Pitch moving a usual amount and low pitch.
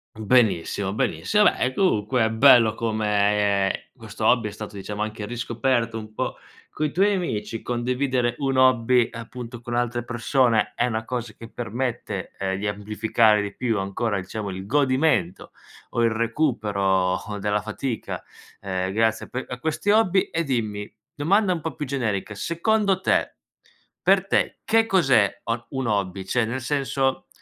Yes: average, 4.1 semitones; low, 115 Hz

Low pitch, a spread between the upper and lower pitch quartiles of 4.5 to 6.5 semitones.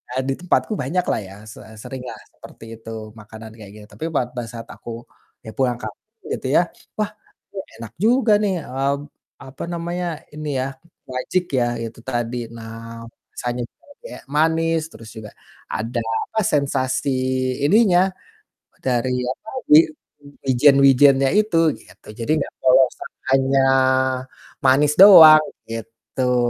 Yes: low, 130 Hz; wide, 5.6 semitones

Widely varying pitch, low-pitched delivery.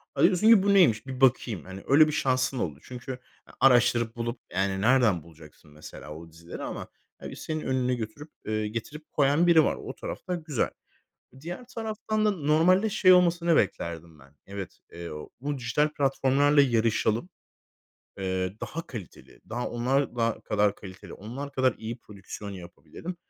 Yes: wide, 7.2 semitones; low, 125 Hz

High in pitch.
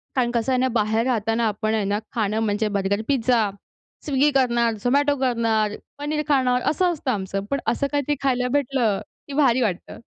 Yes: high, 245 Hz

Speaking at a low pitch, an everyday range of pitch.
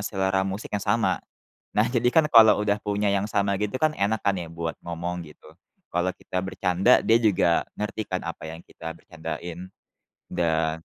Yes: very low, 95 Hz; average, 3.3 semitones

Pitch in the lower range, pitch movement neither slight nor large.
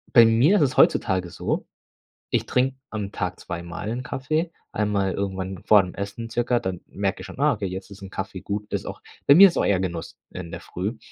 Yes: low, 100 Hz; average, 4.3 semitones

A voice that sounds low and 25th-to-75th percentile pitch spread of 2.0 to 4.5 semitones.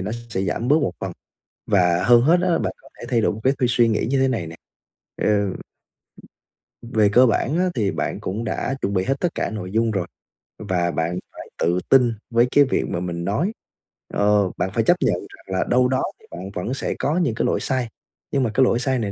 No: low, 115 Hz; average, 5.3 semitones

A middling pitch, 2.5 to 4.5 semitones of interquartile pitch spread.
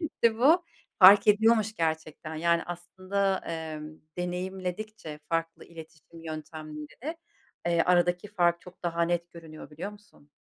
Yes: medium, 175 Hz; average, 3.7 semitones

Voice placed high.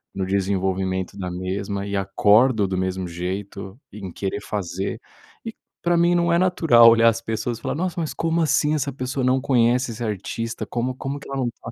No: low, 115 Hz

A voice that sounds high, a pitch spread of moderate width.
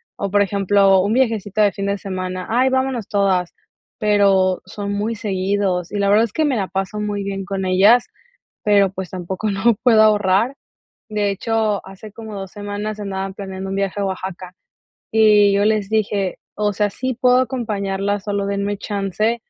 No: high, 200 Hz; narrow, 1.8 semitones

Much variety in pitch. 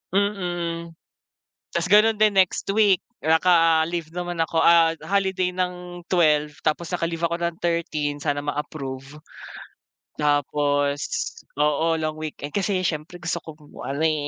No: average, 2.9 semitones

